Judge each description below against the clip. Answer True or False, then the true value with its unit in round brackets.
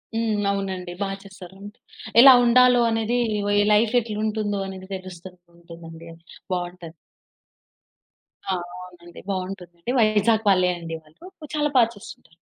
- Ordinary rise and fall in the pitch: True (3.6 semitones)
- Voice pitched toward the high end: True (195 Hz)